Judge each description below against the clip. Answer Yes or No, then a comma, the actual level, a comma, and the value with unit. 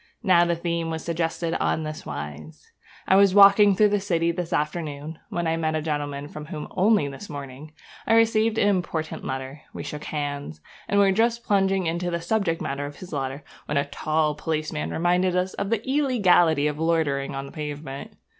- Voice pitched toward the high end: No, medium, 165 Hz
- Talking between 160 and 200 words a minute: Yes, average, 190 wpm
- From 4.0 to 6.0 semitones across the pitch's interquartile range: Yes, average, 4.4 semitones